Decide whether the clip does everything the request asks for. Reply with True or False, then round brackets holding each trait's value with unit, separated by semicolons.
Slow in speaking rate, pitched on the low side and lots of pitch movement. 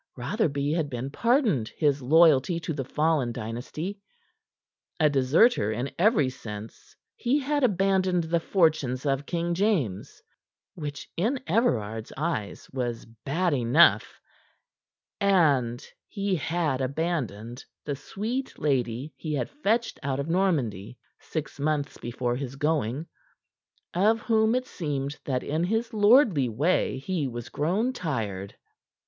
False (125 wpm; 150 Hz; 6.5 semitones)